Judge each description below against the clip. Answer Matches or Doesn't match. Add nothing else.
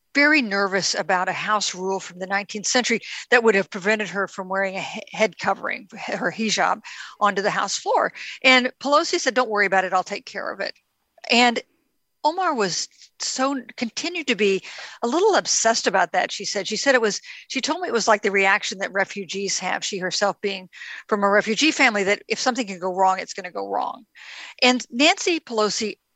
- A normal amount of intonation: Matches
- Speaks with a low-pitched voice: Doesn't match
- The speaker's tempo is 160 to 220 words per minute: Matches